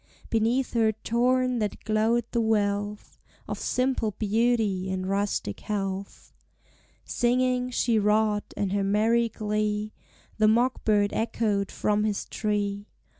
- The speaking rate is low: Yes, slow, 125 wpm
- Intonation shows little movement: Yes, narrow, 2.3 semitones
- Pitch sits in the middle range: No, high, 215 Hz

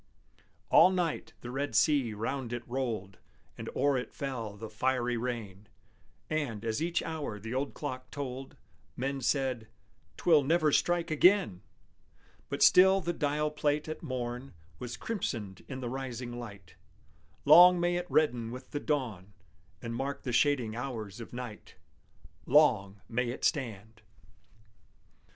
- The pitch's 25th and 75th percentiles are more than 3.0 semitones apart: Yes, average, 4.4 semitones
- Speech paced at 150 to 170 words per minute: No, average, 140 wpm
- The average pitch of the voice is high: No, low, 130 Hz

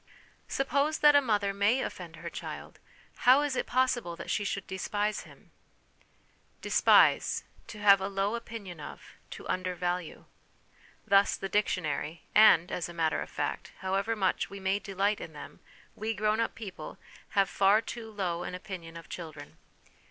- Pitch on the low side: No, high, 200 Hz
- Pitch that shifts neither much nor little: Yes, average, 3.3 semitones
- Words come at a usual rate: Yes, average, 165 wpm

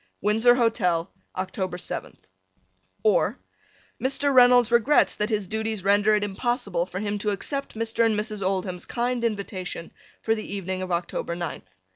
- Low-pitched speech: No, high, 210 Hz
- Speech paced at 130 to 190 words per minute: Yes, average, 150 wpm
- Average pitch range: Yes, average, 3.8 semitones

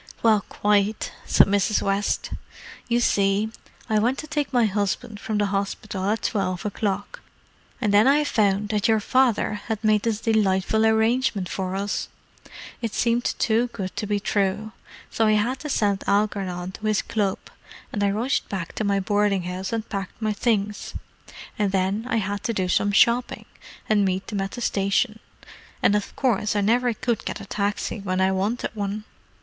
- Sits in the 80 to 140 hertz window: No, high, 210 Hz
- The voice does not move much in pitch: Yes, narrow, 2.1 semitones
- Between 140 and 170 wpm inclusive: No, average, 180 wpm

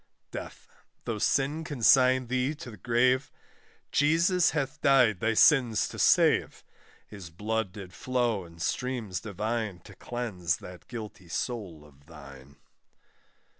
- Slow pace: Yes, slow, 130 wpm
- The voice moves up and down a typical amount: No, wide, 5.9 semitones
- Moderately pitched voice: No, low, 115 Hz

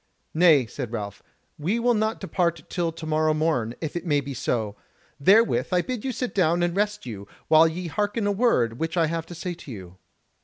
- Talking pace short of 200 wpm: No, fast, 205 wpm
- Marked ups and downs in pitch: Yes, wide, 5.7 semitones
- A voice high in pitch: No, medium, 165 Hz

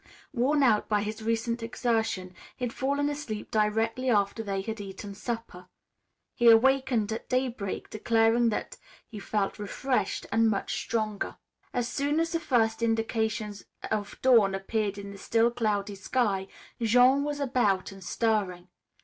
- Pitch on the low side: No, high, 225 Hz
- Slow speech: No, average, 150 wpm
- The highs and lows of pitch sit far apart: No, average, 3.2 semitones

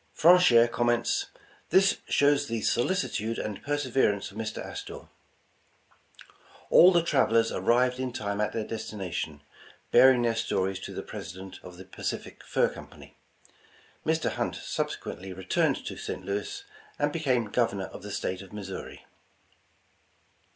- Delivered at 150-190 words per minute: No, slow, 135 wpm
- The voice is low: Yes, low, 115 Hz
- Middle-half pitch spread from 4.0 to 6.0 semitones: Yes, average, 4.9 semitones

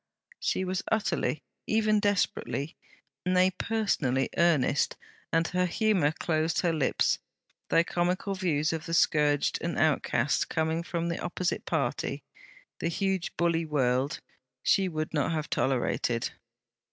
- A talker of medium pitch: Yes, medium, 165 Hz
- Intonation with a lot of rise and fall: No, average, 3.3 semitones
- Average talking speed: No, slow, 130 wpm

